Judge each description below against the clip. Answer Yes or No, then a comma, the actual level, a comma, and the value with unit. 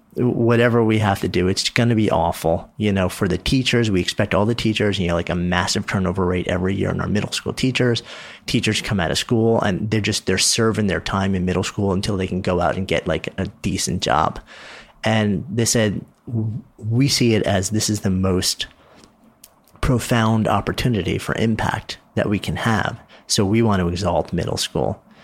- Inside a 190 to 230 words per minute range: Yes, fast, 205 wpm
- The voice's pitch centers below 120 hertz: Yes, low, 105 Hz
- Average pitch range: Yes, average, 3.4 semitones